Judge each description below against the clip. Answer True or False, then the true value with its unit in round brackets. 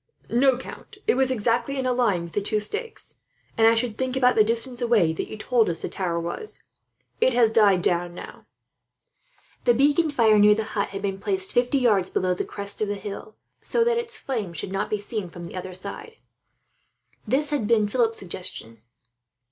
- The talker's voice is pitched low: False (220 Hz)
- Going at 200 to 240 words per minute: True (205 wpm)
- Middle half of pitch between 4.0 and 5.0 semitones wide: True (4.5 semitones)